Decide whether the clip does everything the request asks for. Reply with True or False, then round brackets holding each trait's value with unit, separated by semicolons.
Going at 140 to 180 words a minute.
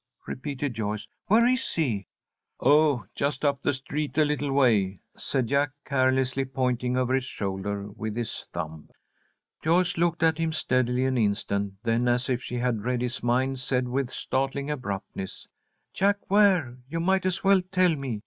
True (165 wpm)